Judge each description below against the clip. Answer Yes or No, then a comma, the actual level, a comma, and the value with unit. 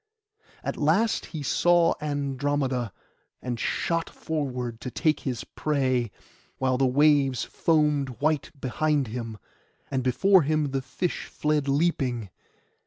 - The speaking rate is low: Yes, slow, 120 wpm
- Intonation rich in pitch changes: No, average, 3.2 semitones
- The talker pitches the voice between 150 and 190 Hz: No, medium, 140 Hz